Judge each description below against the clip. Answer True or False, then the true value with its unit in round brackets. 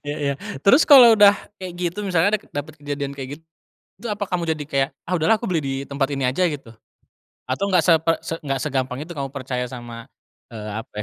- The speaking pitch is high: False (150 Hz)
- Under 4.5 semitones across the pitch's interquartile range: False (5.1 semitones)